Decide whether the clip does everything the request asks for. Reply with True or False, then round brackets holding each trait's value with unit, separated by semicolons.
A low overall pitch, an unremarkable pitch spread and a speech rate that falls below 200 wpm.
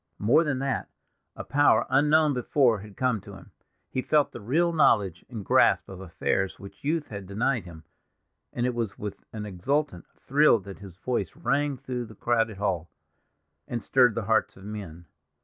False (115 Hz; 5.7 semitones; 180 wpm)